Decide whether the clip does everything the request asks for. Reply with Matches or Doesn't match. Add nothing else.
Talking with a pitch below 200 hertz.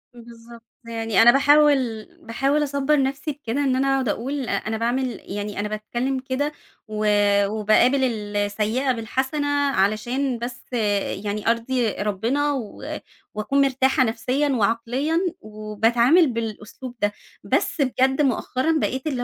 Doesn't match